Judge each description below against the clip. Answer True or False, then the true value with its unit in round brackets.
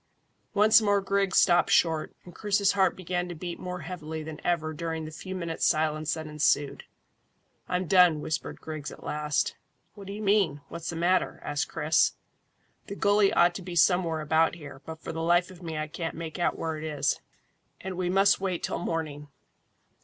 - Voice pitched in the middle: True (170 Hz)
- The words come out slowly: False (190 wpm)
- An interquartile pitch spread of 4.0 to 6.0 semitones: False (2.9 semitones)